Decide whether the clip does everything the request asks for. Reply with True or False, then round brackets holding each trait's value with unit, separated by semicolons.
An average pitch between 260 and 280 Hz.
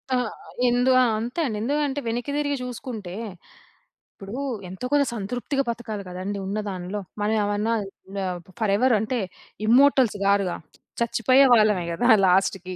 False (220 Hz)